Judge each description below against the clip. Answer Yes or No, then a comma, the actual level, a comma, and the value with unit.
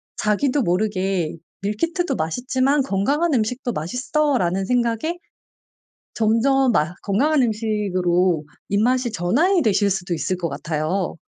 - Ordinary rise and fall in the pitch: No, wide, 6.2 semitones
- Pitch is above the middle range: Yes, high, 215 Hz